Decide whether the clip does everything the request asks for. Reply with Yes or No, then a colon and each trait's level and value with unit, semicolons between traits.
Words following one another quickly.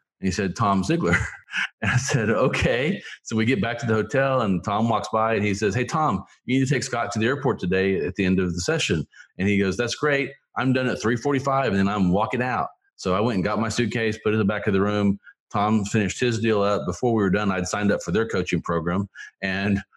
Yes: fast, 260 wpm